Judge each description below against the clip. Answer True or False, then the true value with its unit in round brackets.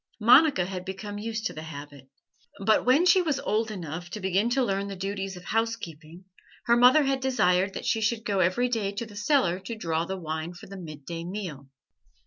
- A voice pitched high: True (195 Hz)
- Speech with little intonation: False (4.6 semitones)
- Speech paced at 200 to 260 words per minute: True (205 wpm)